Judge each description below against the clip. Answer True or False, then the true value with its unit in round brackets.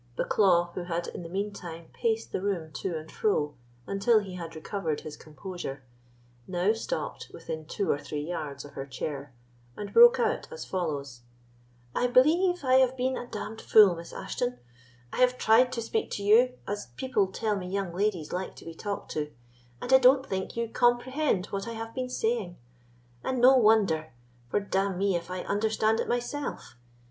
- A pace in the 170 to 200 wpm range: True (185 wpm)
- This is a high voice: True (200 Hz)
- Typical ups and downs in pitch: False (6.0 semitones)